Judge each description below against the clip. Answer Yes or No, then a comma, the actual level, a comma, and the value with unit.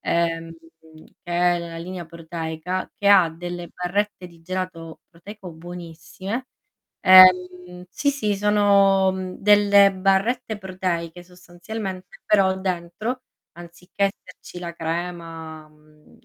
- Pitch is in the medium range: Yes, medium, 180 Hz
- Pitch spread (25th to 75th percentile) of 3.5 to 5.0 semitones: No, narrow, 2.5 semitones